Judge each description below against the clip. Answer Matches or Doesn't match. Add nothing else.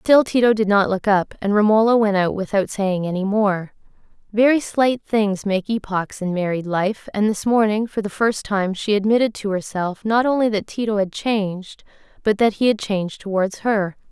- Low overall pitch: Doesn't match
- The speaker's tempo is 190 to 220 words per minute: Matches